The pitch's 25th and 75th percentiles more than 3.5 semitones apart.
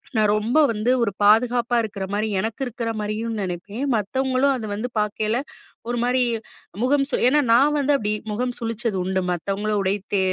No: average, 3.0 semitones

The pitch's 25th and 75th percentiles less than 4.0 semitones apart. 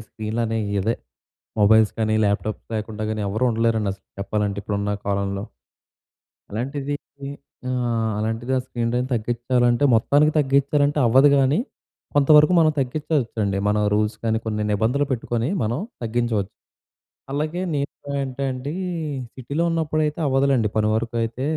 No: average, 4.3 semitones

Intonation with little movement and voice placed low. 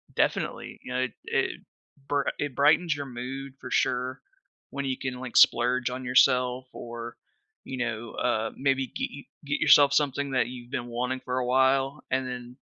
Yes: narrow, 1.7 semitones; low, 130 Hz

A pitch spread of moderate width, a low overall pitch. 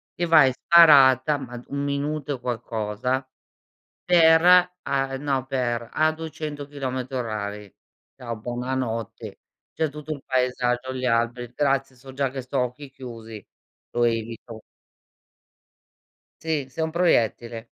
Yes: average, 3.3 semitones; low, 130 Hz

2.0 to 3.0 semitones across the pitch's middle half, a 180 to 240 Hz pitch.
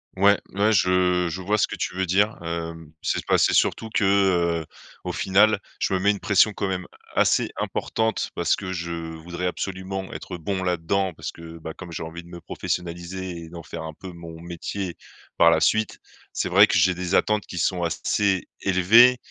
No: narrow, 2.5 semitones; very low, 90 Hz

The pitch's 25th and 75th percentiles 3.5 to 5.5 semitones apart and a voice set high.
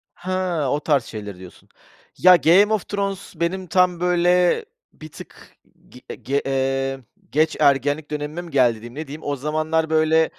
No: average, 4.4 semitones; medium, 155 Hz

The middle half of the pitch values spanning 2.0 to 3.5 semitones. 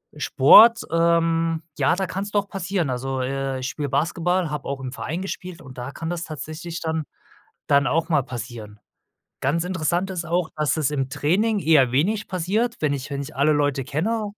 No: average, 4.3 semitones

